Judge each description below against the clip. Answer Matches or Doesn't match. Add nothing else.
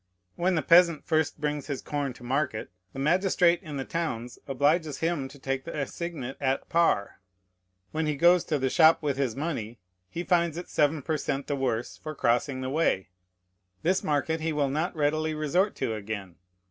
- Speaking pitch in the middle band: Matches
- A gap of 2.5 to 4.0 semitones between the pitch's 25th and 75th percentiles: Matches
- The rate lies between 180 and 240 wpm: Matches